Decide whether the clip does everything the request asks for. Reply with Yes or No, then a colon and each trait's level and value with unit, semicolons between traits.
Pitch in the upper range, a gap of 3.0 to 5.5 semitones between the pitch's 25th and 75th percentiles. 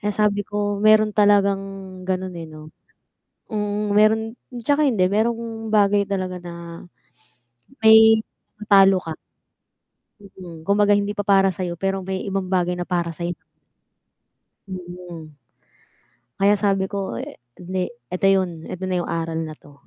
No: high, 195 Hz; narrow, 2.6 semitones